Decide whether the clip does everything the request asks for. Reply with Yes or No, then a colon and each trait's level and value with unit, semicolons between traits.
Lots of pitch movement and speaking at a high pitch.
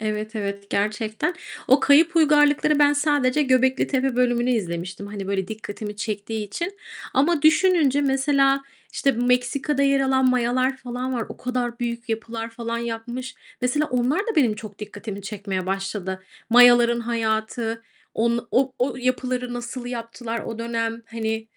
No: average, 3.2 semitones; high, 240 Hz